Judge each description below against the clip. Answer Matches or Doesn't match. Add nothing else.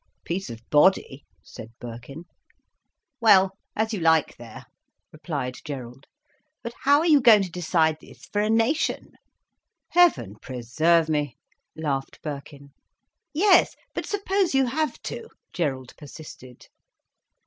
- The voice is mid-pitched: Matches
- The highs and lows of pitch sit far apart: Matches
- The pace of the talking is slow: Matches